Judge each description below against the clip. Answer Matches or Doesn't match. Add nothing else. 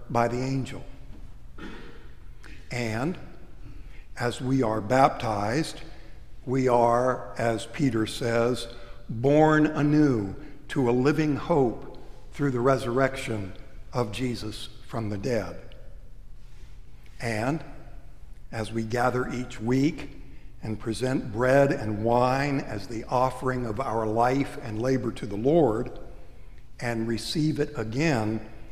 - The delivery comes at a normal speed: Doesn't match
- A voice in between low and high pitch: Doesn't match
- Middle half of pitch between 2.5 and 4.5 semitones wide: Matches